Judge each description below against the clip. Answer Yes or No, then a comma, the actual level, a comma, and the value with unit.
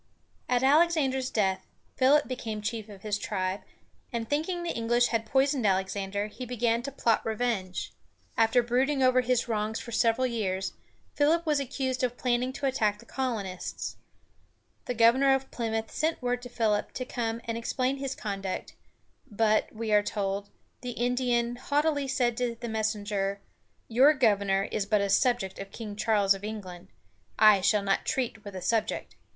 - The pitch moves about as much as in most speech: Yes, average, 3.6 semitones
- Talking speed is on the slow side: No, average, 165 wpm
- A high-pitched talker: Yes, high, 230 Hz